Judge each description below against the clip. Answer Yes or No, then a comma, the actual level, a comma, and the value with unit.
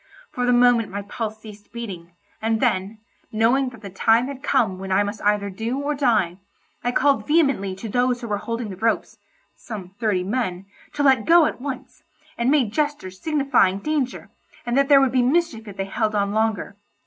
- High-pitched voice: Yes, high, 225 Hz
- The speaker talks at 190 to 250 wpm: Yes, average, 195 wpm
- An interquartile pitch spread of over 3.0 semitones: Yes, average, 4.6 semitones